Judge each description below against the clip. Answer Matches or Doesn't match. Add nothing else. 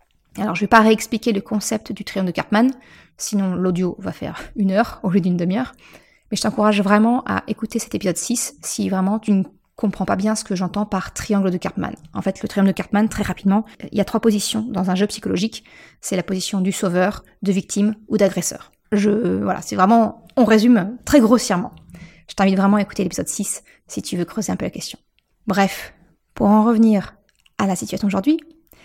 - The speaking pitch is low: Doesn't match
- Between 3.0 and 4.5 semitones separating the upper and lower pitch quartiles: Doesn't match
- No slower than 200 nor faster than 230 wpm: Matches